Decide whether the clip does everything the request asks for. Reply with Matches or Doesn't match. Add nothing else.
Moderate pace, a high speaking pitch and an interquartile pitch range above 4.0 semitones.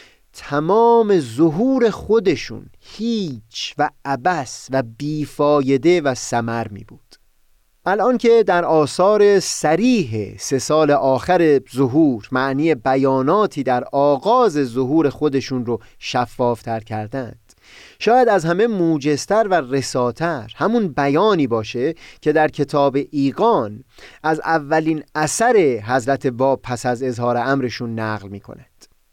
Doesn't match